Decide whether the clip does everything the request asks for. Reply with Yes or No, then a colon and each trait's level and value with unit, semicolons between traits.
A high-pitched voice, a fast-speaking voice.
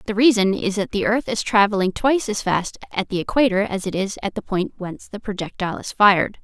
Yes: high, 200 Hz; fast, 235 wpm